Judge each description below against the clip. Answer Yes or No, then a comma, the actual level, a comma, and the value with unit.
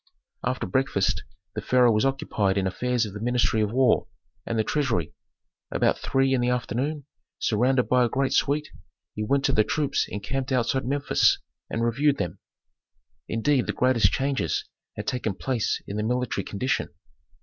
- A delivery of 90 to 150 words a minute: No, average, 165 wpm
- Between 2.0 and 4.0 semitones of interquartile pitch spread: Yes, average, 3.6 semitones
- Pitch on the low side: Yes, low, 125 Hz